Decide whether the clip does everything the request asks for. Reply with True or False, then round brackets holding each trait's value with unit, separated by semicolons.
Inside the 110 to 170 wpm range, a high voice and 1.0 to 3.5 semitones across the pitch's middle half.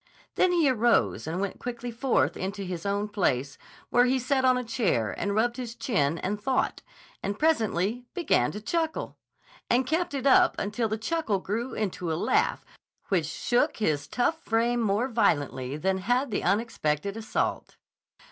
False (165 wpm; 220 Hz; 4.9 semitones)